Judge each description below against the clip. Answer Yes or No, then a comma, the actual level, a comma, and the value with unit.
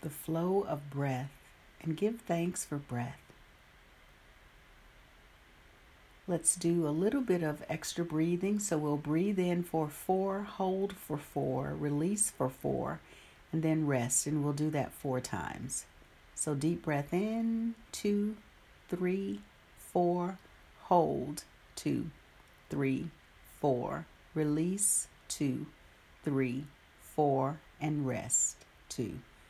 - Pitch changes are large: No, average, 4.5 semitones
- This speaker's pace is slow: Yes, slow, 115 wpm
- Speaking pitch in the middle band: Yes, medium, 155 Hz